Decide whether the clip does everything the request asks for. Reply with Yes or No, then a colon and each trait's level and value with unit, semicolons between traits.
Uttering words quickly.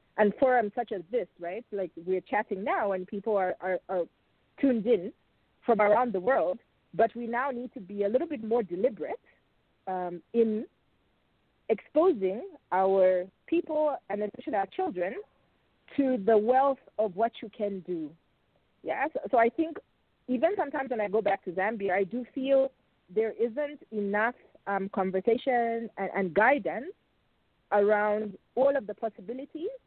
No: average, 155 wpm